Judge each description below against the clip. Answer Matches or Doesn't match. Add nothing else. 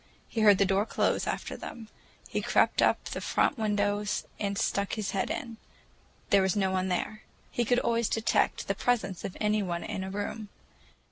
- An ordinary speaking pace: Matches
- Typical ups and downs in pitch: Doesn't match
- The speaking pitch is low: Doesn't match